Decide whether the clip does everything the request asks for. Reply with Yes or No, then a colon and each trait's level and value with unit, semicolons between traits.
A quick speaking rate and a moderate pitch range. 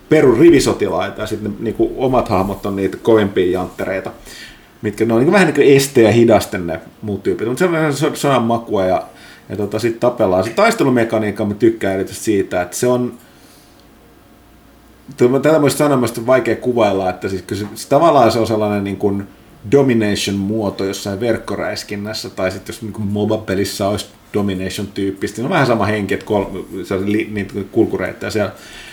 Yes: fast, 170 wpm; average, 3.2 semitones